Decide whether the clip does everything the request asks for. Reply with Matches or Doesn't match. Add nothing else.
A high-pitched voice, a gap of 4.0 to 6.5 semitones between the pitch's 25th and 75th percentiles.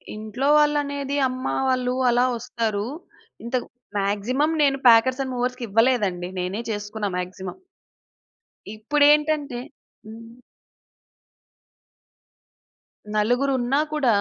Matches